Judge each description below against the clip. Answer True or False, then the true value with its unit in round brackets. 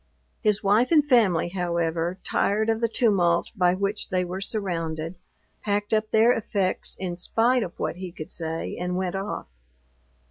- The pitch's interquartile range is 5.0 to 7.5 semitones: False (3.7 semitones)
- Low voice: False (190 Hz)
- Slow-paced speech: False (165 wpm)